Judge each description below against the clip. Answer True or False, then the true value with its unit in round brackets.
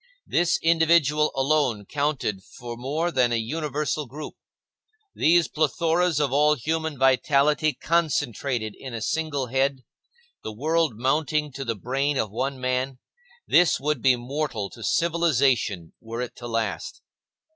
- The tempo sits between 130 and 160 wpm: True (135 wpm)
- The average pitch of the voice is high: False (140 Hz)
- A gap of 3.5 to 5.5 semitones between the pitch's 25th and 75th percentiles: True (4.1 semitones)